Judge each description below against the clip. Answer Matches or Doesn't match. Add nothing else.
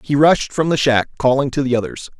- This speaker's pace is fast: Matches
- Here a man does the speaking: Matches